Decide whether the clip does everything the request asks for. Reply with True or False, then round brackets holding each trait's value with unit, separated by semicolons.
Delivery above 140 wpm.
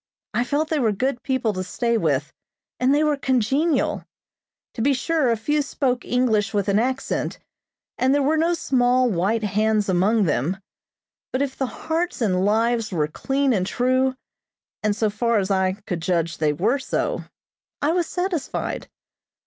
True (170 wpm)